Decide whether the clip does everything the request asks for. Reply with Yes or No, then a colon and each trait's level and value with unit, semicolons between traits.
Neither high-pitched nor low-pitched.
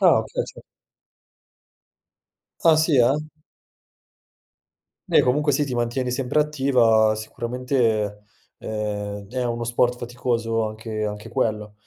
No: low, 120 Hz